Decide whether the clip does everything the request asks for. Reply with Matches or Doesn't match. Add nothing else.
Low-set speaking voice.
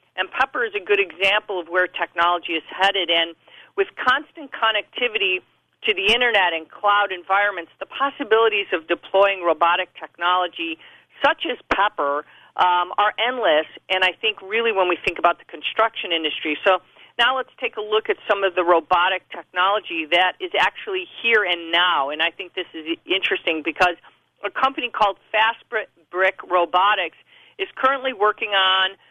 Doesn't match